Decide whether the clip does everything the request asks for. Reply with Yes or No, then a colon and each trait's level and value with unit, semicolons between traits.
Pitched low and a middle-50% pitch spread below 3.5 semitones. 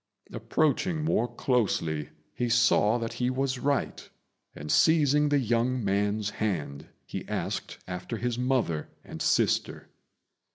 No: low, 120 Hz; average, 4.6 semitones